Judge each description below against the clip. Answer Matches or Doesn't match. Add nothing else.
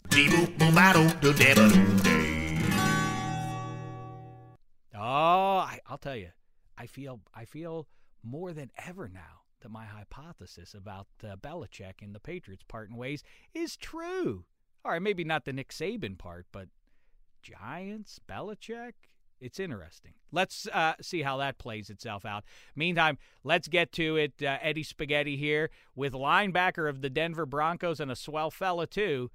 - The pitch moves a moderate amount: Doesn't match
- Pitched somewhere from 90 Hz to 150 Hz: Matches